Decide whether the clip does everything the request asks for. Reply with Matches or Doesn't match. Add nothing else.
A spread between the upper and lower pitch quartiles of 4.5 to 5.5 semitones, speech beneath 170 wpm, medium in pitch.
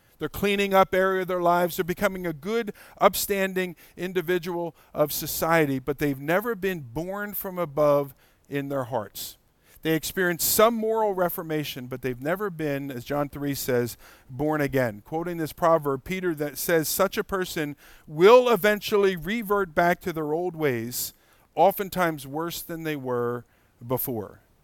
Matches